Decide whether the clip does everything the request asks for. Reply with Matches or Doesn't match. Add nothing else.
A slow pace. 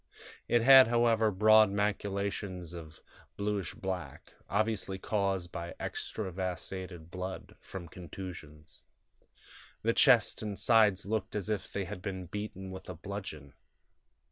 Matches